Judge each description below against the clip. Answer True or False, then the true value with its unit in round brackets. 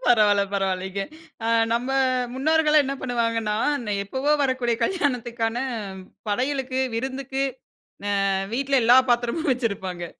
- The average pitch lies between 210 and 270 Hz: True (245 Hz)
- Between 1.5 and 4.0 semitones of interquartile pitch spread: True (3.3 semitones)